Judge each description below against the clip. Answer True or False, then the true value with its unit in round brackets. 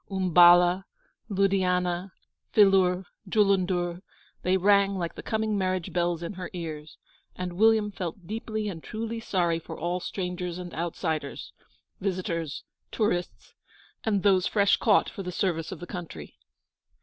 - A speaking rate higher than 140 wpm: False (135 wpm)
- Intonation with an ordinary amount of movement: False (2.3 semitones)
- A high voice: False (180 Hz)